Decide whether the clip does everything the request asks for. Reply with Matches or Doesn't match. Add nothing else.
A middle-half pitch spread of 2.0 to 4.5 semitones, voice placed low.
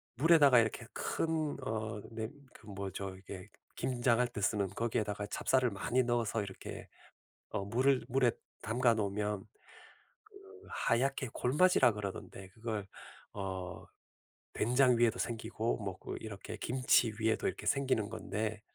Matches